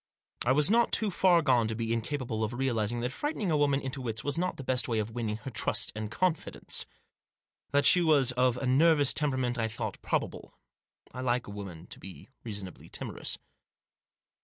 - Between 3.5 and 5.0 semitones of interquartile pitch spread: Yes, average, 4.4 semitones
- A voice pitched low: Yes, low, 125 Hz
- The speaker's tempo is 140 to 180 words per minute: No, average, 190 wpm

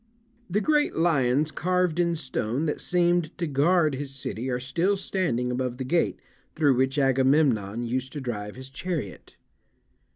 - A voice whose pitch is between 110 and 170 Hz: Yes, medium, 140 Hz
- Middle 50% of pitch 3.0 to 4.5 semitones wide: No, average, 5.0 semitones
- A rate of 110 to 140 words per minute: No, average, 155 wpm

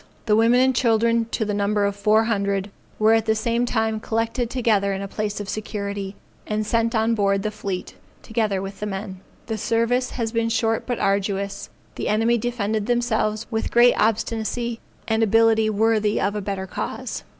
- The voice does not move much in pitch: Yes, narrow, 2.1 semitones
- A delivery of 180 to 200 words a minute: Yes, average, 185 wpm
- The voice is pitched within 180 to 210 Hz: No, high, 220 Hz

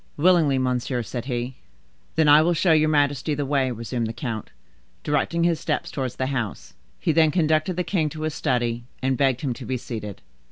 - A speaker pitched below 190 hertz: Yes, medium, 140 Hz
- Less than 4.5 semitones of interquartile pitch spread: Yes, average, 4.0 semitones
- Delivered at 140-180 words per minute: No, average, 200 wpm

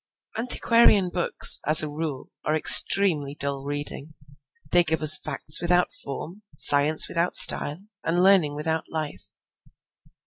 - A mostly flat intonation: No, average, 3.3 semitones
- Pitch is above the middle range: No, medium, 155 Hz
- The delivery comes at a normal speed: No, slow, 130 wpm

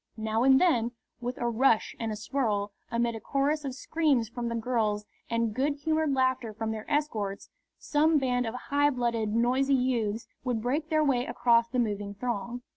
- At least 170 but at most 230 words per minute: Yes, average, 185 wpm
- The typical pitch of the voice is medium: No, high, 240 Hz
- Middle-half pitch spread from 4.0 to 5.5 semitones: No, average, 3.4 semitones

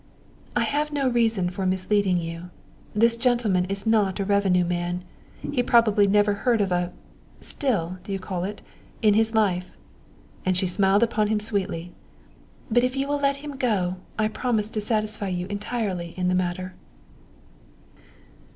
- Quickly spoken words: No, average, 165 wpm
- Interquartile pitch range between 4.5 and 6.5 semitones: No, average, 3.8 semitones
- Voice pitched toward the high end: Yes, high, 205 Hz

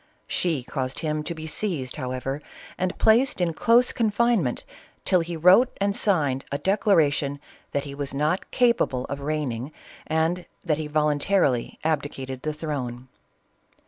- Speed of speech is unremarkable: Yes, average, 145 wpm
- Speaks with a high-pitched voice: No, medium, 155 Hz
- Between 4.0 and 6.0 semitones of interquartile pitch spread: Yes, average, 4.7 semitones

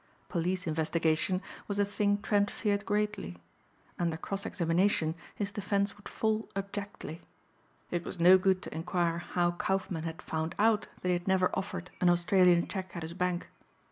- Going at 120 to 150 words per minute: No, average, 165 wpm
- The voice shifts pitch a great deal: No, average, 2.9 semitones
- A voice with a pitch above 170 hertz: Yes, medium, 185 Hz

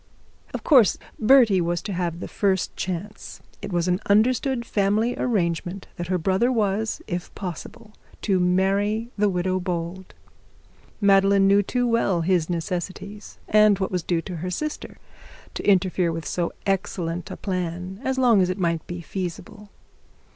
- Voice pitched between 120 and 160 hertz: No, high, 190 Hz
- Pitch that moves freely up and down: No, average, 2.9 semitones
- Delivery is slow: No, average, 155 wpm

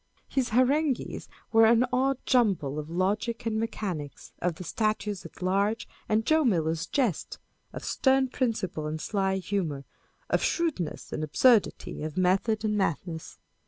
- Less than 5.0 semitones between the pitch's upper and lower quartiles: No, wide, 5.6 semitones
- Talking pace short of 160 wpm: Yes, average, 145 wpm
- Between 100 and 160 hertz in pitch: No, high, 210 Hz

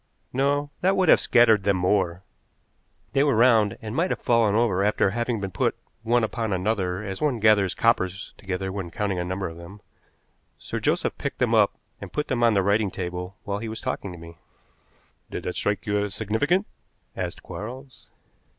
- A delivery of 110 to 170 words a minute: No, average, 190 wpm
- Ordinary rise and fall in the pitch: Yes, average, 3.7 semitones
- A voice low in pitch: Yes, low, 105 Hz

